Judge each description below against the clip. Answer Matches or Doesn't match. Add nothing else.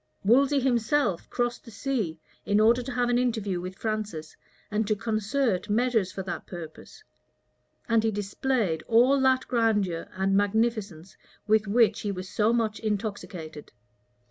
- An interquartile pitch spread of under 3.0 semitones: Doesn't match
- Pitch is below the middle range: Doesn't match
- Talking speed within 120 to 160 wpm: Matches